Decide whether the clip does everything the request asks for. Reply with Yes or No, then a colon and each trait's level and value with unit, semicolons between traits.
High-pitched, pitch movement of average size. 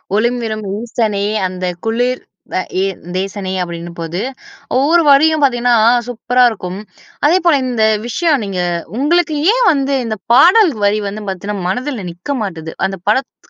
No: high, 230 Hz; wide, 6.1 semitones